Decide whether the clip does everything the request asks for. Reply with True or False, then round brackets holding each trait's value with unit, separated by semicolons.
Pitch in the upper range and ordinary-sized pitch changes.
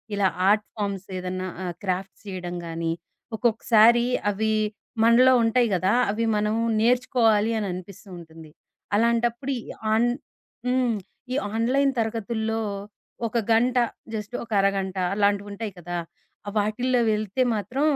True (215 Hz; 3.2 semitones)